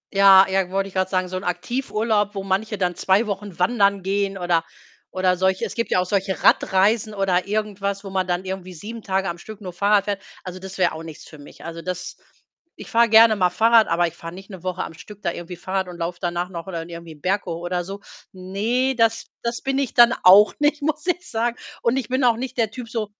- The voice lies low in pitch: No, high, 195 Hz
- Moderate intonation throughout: Yes, average, 3.2 semitones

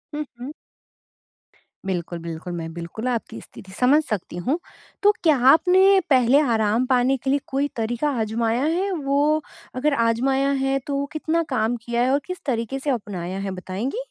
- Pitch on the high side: Yes, very high, 255 Hz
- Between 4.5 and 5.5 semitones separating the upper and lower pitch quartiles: Yes, average, 5.0 semitones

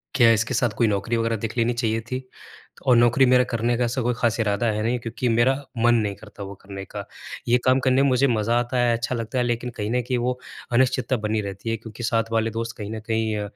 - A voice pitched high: No, low, 115 Hz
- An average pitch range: No, narrow, 1.9 semitones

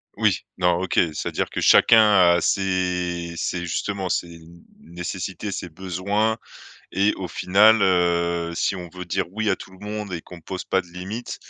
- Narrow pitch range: Yes, narrow, 2.2 semitones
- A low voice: Yes, very low, 90 Hz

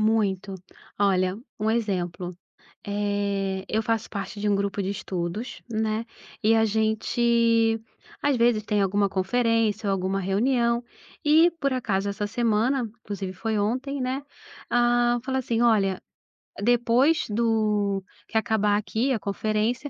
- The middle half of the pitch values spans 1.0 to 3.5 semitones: Yes, average, 2.8 semitones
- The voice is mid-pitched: No, high, 220 Hz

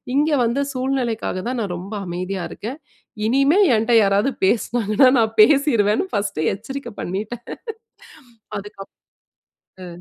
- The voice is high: Yes, high, 225 Hz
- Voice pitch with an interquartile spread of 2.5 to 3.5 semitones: No, average, 4.5 semitones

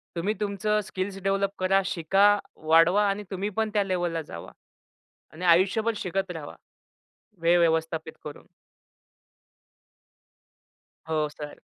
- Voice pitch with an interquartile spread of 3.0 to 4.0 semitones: Yes, average, 3.4 semitones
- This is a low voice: No, medium, 185 Hz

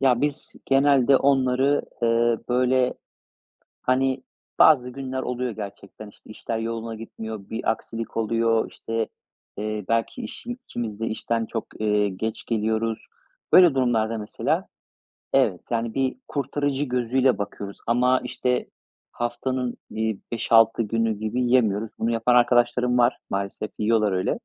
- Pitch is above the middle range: No, low, 115 Hz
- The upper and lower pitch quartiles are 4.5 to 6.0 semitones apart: No, narrow, 2.4 semitones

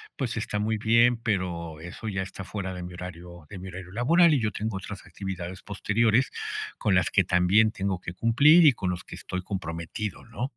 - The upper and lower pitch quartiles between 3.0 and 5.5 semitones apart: Yes, average, 3.7 semitones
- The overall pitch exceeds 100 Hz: No, very low, 95 Hz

